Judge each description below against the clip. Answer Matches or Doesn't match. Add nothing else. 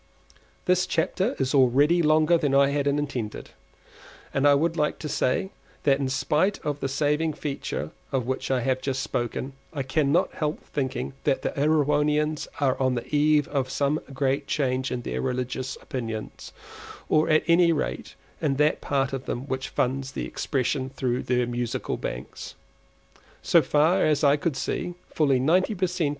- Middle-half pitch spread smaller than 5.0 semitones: Matches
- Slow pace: Doesn't match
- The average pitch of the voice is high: Doesn't match